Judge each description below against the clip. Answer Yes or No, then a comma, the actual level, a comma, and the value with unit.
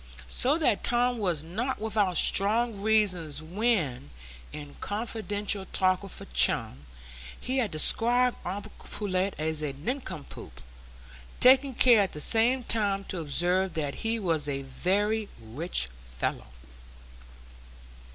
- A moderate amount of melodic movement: No, wide, 6.2 semitones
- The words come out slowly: Yes, slow, 125 wpm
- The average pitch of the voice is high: Yes, high, 195 Hz